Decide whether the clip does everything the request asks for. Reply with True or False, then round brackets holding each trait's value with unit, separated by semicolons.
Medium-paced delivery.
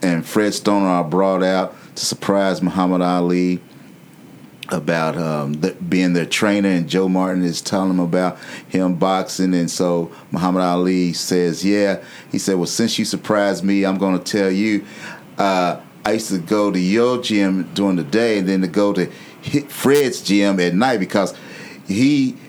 True (175 wpm)